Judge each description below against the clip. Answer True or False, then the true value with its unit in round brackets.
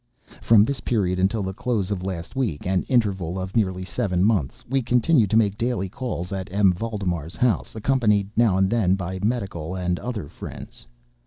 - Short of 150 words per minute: False (170 wpm)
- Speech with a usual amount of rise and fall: True (3.8 semitones)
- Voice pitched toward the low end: True (100 Hz)